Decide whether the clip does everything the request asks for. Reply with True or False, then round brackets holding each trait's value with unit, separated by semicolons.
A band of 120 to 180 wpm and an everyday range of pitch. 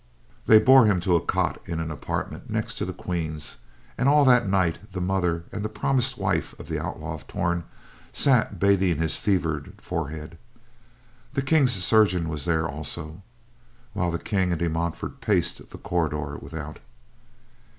True (160 wpm; 4.5 semitones)